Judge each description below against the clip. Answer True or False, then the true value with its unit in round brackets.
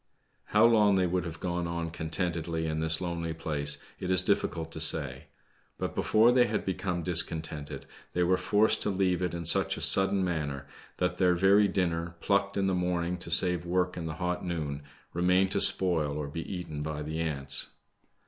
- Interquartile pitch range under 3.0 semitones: True (2.5 semitones)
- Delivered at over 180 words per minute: True (190 wpm)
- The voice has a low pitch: True (85 Hz)